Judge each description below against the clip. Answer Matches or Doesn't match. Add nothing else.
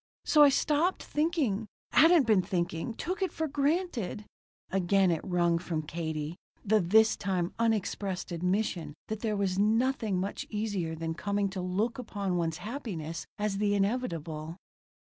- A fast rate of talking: Doesn't match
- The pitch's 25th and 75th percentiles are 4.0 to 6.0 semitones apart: Matches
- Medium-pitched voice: Doesn't match